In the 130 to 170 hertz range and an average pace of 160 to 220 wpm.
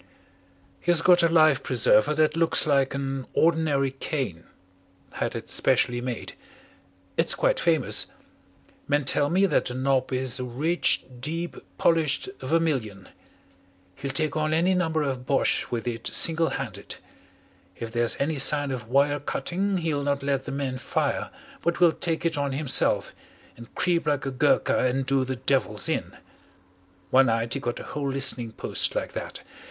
Yes: medium, 140 Hz; average, 165 wpm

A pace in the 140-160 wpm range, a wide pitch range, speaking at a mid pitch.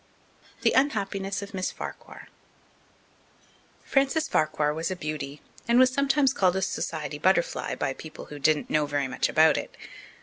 Yes: average, 155 wpm; wide, 7.0 semitones; medium, 180 Hz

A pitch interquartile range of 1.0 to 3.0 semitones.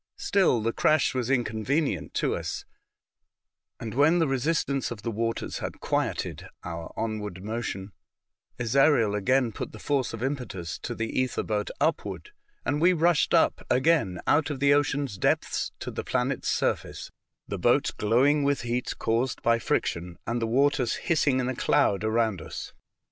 No: average, 4.4 semitones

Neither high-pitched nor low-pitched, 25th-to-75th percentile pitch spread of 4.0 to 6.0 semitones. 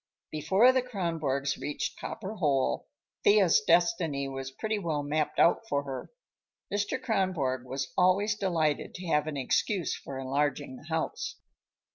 Yes: medium, 155 Hz; wide, 5.5 semitones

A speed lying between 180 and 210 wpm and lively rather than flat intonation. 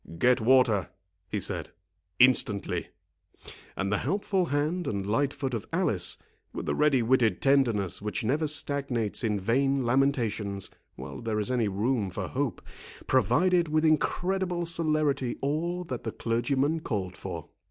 No: average, 140 wpm; wide, 6.0 semitones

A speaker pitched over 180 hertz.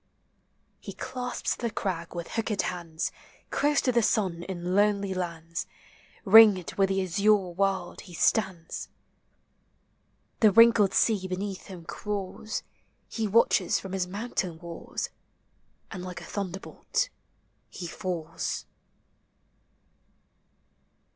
Yes: high, 190 Hz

